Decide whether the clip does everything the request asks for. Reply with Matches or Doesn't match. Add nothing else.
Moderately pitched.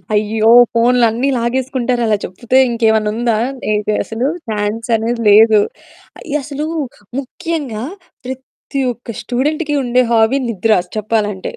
Doesn't match